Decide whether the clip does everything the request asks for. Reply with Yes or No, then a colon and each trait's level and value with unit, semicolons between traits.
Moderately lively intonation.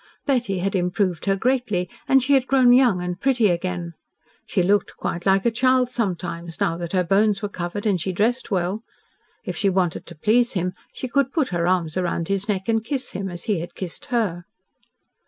Yes: average, 5.0 semitones